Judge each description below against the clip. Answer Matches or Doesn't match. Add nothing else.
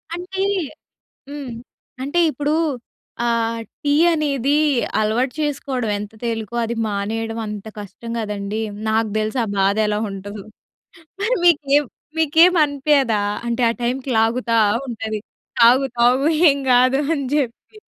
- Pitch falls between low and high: Doesn't match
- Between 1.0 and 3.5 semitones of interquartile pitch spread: Doesn't match